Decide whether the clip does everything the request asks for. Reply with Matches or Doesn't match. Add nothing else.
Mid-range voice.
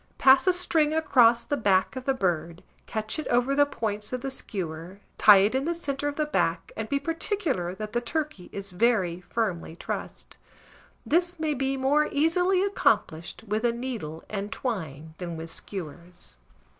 Doesn't match